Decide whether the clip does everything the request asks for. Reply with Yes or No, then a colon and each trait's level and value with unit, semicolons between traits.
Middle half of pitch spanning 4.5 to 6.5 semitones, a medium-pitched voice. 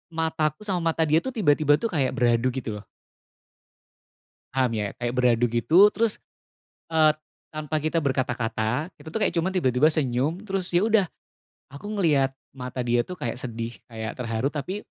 Yes: wide, 5.5 semitones; medium, 145 Hz